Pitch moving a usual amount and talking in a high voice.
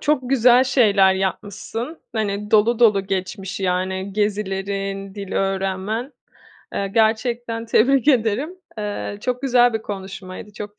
Yes: average, 3.5 semitones; high, 210 Hz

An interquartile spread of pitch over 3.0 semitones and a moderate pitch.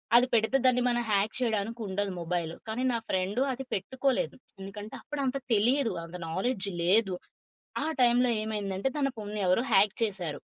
No: average, 4.2 semitones; high, 215 Hz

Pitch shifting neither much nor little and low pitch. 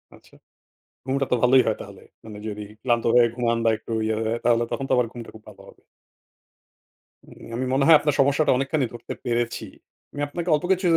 Yes: average, 3.1 semitones; low, 125 Hz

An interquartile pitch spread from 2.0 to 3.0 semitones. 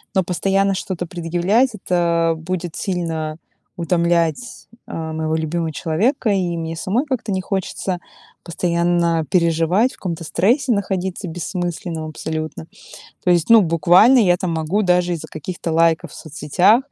Yes: narrow, 2.6 semitones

